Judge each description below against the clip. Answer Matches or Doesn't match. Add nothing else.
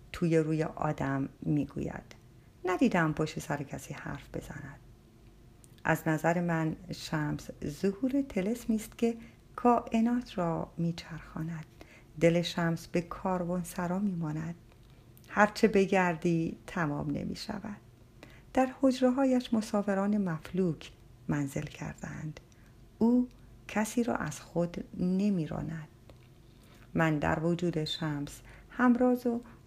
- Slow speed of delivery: Matches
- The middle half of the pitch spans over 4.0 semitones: Matches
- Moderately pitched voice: Matches